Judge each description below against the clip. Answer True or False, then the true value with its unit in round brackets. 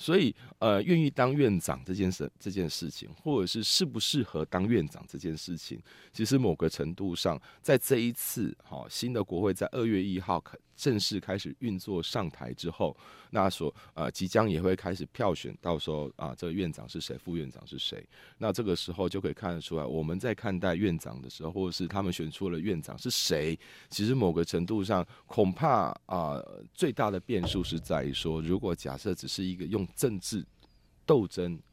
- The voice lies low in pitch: True (90 Hz)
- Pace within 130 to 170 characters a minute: False (295 characters per minute)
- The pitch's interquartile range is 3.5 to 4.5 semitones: True (4.2 semitones)